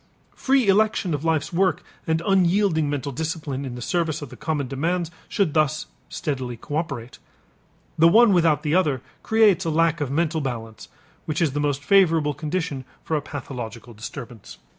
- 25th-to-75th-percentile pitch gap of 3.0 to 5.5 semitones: Yes, average, 3.5 semitones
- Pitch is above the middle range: No, medium, 155 Hz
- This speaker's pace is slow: No, average, 165 wpm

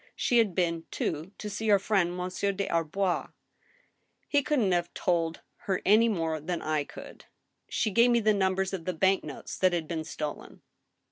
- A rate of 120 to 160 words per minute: No, average, 190 wpm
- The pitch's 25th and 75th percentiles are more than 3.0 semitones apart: Yes, average, 3.5 semitones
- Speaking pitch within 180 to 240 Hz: Yes, medium, 185 Hz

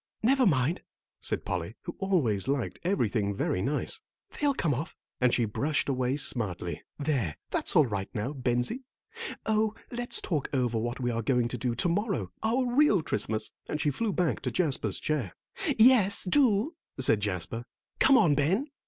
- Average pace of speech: Yes, average, 170 wpm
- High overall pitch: No, medium, 140 Hz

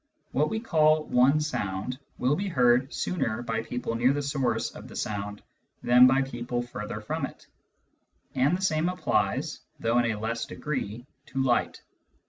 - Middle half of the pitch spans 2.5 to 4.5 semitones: Yes, average, 4.2 semitones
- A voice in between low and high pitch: No, low, 125 Hz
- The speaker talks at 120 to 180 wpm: Yes, average, 165 wpm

